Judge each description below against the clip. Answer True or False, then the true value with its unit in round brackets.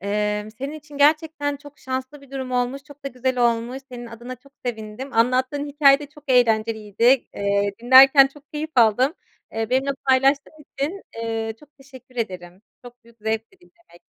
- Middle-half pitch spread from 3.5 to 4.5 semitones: True (3.8 semitones)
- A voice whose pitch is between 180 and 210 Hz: False (255 Hz)